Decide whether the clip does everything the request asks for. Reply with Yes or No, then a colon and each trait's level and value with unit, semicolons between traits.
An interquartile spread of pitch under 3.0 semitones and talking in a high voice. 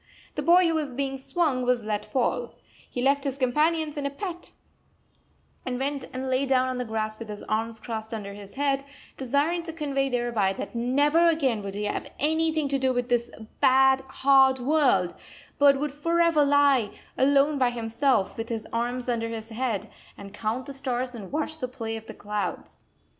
No: average, 3.9 semitones; very high, 260 Hz